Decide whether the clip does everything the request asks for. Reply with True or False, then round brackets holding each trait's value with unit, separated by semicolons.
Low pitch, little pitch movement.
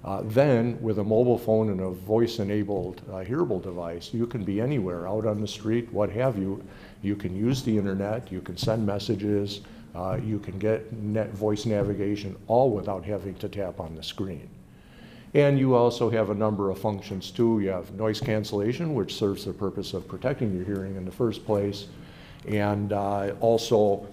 True (105 Hz; 2.3 semitones)